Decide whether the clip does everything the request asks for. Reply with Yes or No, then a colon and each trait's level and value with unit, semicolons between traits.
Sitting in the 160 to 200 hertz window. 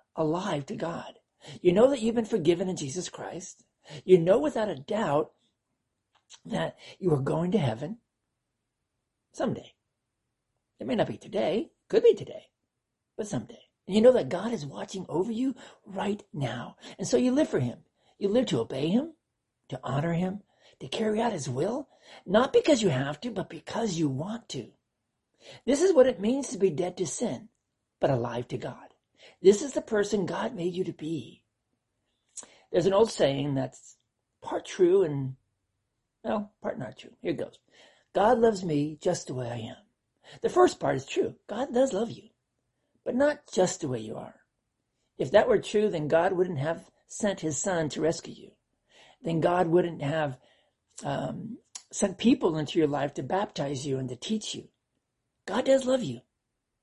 Yes: medium, 185 Hz